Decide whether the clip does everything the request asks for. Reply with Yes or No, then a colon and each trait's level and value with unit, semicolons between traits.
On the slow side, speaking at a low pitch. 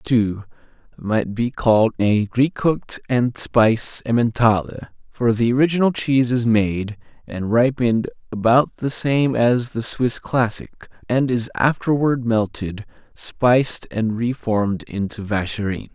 Yes: slow, 130 wpm; low, 115 Hz